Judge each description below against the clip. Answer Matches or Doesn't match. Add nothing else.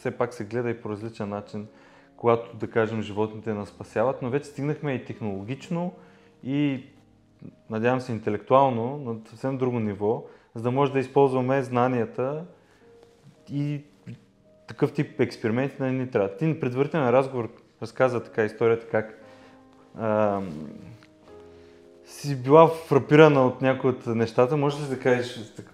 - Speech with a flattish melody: Doesn't match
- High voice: Doesn't match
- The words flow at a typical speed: Matches